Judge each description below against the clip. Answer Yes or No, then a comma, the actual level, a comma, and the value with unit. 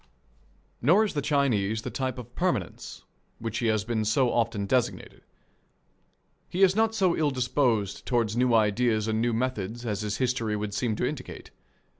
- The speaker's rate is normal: Yes, average, 170 wpm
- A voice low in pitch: Yes, low, 120 Hz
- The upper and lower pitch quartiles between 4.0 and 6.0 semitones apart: No, average, 3.3 semitones